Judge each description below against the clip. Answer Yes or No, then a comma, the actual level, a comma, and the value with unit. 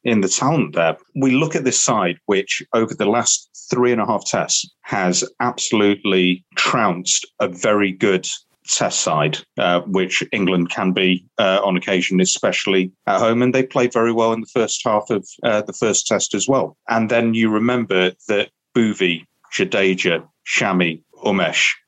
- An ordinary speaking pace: Yes, average, 170 wpm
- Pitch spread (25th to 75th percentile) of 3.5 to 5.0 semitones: Yes, average, 4.1 semitones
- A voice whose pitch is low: Yes, low, 100 Hz